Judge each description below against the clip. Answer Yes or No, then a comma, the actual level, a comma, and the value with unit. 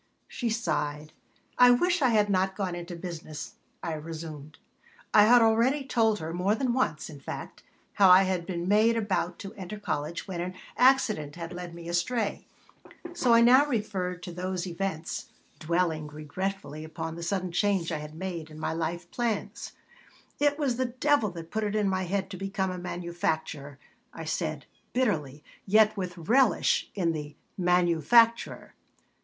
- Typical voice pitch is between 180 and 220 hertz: Yes, medium, 185 Hz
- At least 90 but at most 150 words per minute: No, average, 165 wpm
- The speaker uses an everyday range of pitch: Yes, average, 4.6 semitones